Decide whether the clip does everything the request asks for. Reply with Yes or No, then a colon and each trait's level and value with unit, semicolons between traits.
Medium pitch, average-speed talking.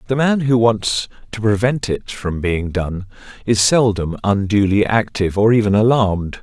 No: low, 105 Hz; average, 160 wpm